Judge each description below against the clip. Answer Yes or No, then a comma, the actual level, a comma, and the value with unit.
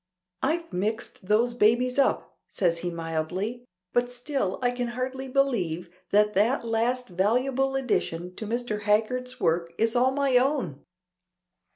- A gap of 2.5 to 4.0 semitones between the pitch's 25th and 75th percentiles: No, average, 4.9 semitones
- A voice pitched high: Yes, high, 235 Hz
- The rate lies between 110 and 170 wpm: Yes, average, 140 wpm